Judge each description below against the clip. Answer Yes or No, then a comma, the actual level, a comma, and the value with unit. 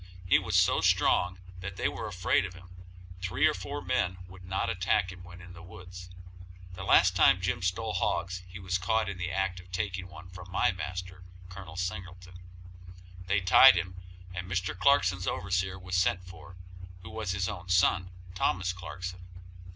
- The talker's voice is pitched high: No, very low, 90 Hz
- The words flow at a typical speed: Yes, average, 180 wpm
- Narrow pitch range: Yes, narrow, 0.7 semitones